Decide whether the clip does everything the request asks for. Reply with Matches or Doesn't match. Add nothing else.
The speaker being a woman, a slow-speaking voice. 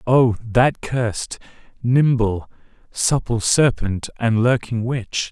Doesn't match